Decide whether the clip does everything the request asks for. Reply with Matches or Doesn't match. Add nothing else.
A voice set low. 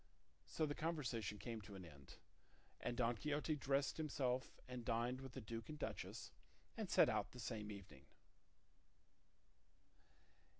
Matches